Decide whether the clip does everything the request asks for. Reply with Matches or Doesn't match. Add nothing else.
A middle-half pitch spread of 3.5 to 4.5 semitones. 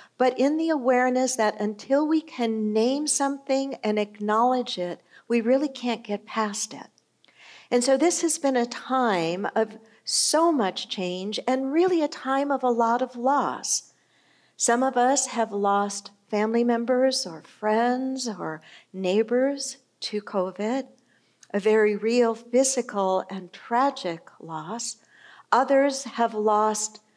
Matches